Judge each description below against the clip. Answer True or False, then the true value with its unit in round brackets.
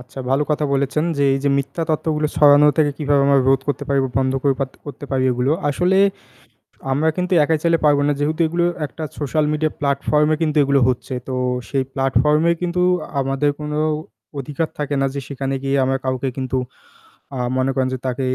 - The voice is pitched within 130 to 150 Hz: True (140 Hz)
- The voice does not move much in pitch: True (2.1 semitones)